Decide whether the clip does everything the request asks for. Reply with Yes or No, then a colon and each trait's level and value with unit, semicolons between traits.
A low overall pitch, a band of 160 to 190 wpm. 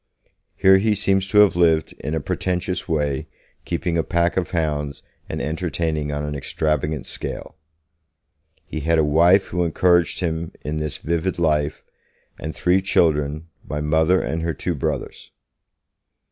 No: very low, 80 Hz; average, 150 wpm